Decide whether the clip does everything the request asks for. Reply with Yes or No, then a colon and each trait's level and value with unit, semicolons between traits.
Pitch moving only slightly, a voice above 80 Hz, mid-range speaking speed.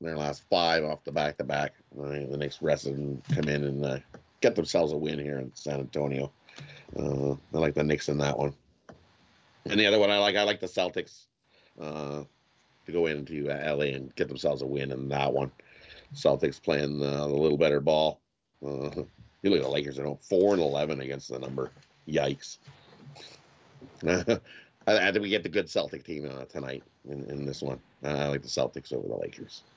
No: narrow, 1.0 semitones; very low, 70 Hz; average, 195 wpm